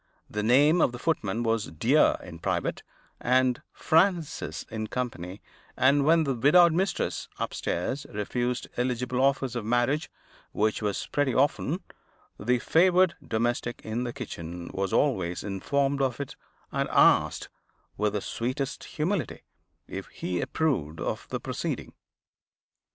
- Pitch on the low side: Yes, low, 125 Hz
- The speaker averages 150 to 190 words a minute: No, slow, 135 wpm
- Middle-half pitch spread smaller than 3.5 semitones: No, average, 4.9 semitones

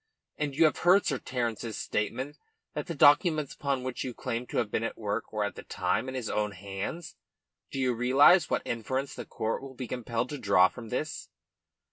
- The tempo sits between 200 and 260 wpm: Yes, fast, 205 wpm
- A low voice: Yes, low, 125 Hz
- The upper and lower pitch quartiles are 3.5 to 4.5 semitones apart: Yes, average, 4.1 semitones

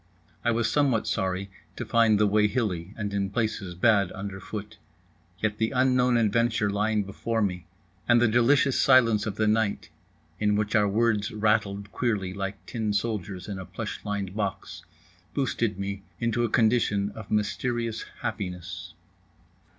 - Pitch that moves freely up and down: No, narrow, 2.6 semitones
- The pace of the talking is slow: No, average, 150 wpm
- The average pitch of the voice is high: No, low, 105 Hz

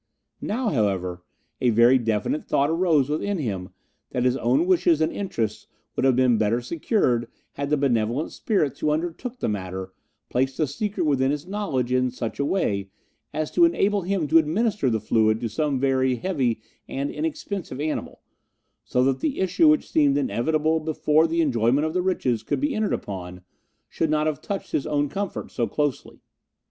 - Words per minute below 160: No, average, 180 wpm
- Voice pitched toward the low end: No, medium, 145 Hz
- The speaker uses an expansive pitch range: Yes, wide, 6.2 semitones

